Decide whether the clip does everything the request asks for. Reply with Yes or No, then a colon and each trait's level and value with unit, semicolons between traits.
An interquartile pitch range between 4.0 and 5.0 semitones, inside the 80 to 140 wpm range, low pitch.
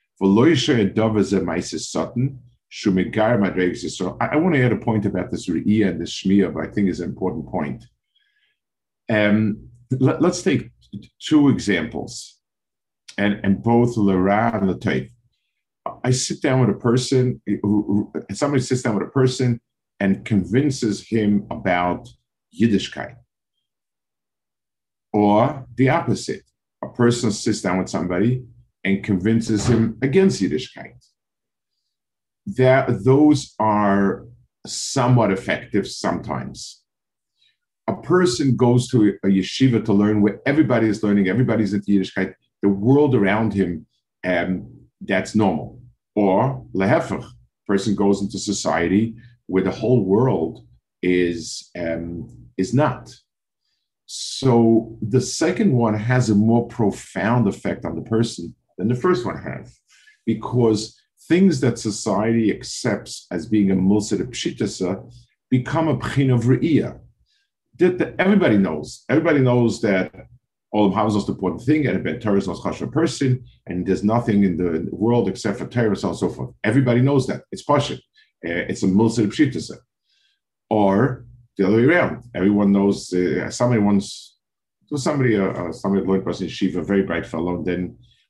Yes: average, 4.3 semitones; slow, 135 wpm; low, 110 Hz